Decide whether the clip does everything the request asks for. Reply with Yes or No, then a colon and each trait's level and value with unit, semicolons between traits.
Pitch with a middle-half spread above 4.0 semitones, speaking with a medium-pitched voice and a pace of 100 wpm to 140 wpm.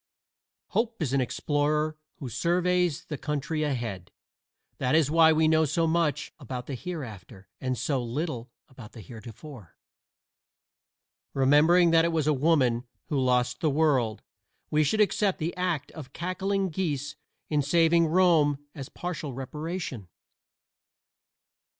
Yes: average, 4.4 semitones; medium, 150 Hz; slow, 135 wpm